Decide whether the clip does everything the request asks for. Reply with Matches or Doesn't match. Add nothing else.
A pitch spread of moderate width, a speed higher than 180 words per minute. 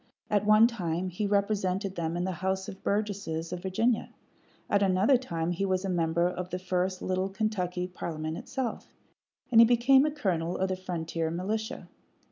Doesn't match